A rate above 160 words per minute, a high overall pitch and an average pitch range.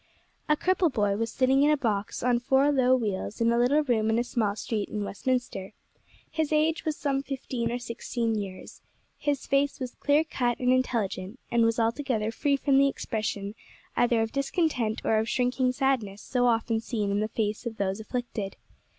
Yes: average, 190 wpm; high, 240 Hz; average, 3.7 semitones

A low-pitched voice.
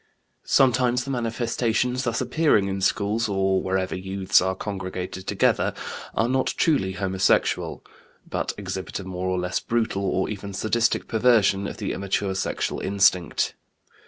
Yes: low, 100 Hz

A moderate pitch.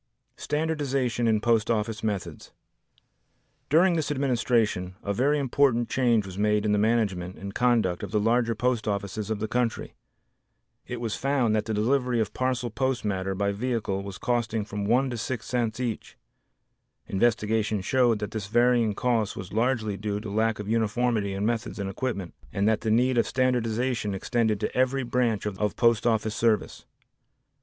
No: low, 115 Hz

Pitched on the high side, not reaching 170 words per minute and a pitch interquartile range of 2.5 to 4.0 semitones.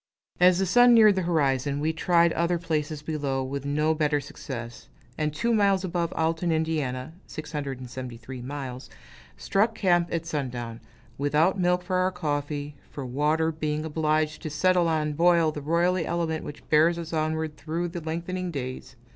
No: medium, 155 Hz; average, 160 wpm; average, 3.1 semitones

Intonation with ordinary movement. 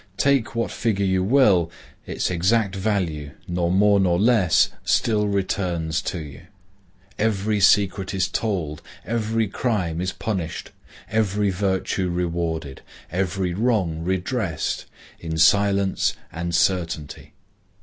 Yes: average, 3.4 semitones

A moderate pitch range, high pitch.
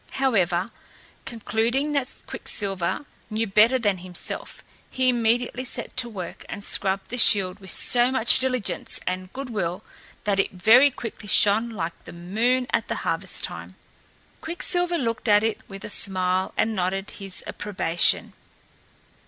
Yes: average, 4.5 semitones; high, 215 Hz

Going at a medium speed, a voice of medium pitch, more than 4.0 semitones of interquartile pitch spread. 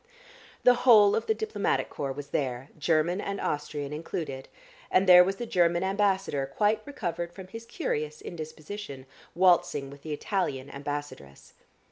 Yes: average, 145 wpm; medium, 170 Hz; wide, 5.5 semitones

